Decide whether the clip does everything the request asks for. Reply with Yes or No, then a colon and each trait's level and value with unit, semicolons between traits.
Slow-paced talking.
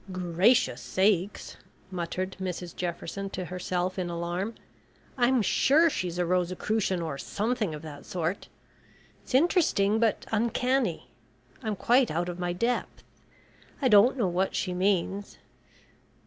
Yes: slow, 130 wpm